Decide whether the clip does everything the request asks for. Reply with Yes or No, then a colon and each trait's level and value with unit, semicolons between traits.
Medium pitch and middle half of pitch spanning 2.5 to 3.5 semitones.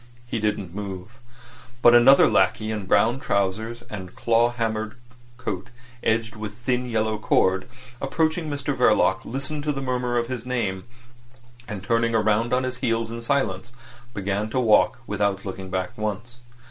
No: low, 115 Hz; average, 3.2 semitones